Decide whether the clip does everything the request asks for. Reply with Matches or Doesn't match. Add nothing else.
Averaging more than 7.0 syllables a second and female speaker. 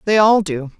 Doesn't match